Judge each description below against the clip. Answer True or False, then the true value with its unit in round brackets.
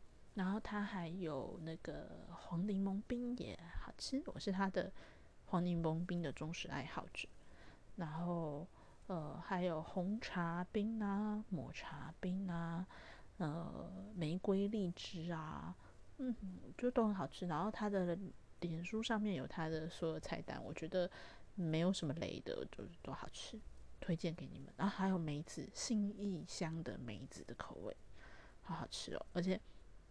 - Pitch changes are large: False (3.3 semitones)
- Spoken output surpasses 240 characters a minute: False (215 characters per minute)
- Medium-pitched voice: True (180 Hz)